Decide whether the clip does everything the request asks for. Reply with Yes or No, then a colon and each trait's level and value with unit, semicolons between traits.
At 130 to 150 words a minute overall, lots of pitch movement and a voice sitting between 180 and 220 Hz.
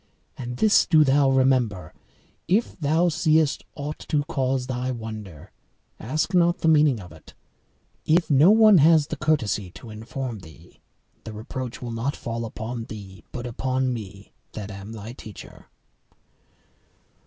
No: average, 145 wpm; wide, 5.8 semitones; low, 130 Hz